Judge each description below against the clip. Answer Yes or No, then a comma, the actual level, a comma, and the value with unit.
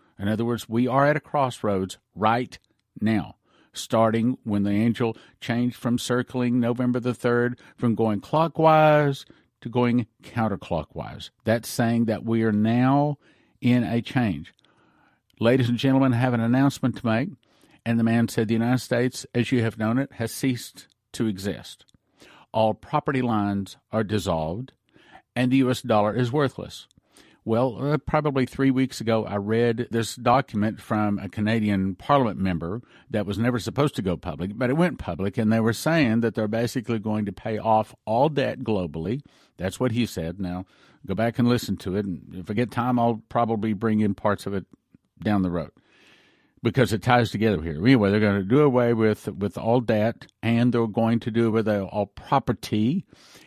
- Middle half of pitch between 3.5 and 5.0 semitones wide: No, average, 2.9 semitones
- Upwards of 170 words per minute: Yes, average, 180 wpm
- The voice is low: Yes, low, 115 Hz